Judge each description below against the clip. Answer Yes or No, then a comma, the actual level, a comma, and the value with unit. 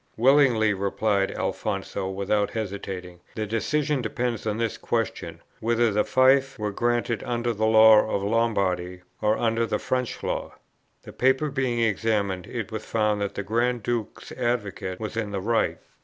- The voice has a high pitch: No, low, 110 Hz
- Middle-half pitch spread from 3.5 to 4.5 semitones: No, average, 2.9 semitones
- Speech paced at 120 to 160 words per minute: Yes, average, 155 wpm